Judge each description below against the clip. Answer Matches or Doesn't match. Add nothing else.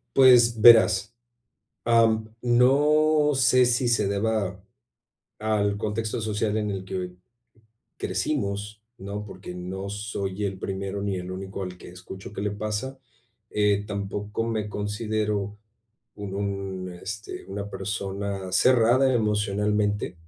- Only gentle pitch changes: Matches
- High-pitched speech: Doesn't match